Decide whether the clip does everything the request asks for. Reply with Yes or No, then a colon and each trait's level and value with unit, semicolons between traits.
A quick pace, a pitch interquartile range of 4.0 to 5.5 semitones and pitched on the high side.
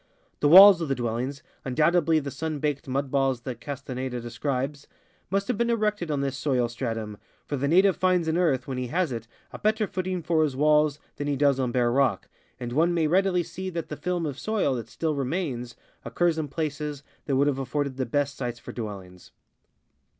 No: fast, 210 wpm; average, 4.5 semitones; medium, 145 Hz